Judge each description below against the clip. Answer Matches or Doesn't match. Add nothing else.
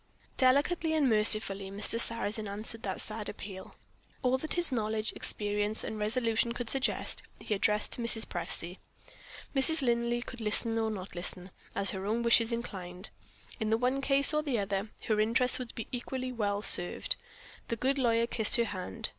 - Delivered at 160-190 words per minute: Matches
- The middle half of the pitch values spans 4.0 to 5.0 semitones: Doesn't match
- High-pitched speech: Matches